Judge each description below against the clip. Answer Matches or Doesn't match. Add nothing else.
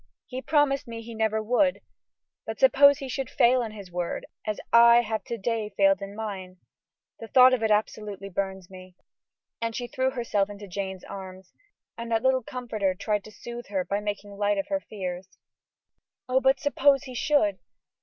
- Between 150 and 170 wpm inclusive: Doesn't match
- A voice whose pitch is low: Doesn't match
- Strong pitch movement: Doesn't match